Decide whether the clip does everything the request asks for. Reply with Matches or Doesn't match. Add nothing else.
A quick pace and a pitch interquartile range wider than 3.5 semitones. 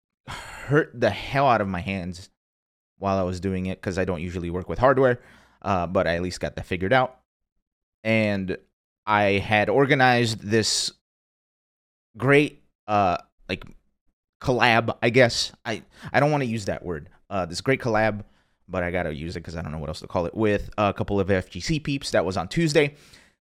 Doesn't match